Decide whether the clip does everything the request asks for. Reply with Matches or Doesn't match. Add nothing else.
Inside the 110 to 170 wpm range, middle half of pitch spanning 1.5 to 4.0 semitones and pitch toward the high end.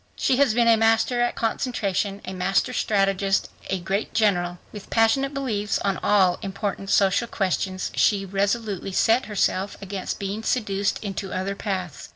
Matches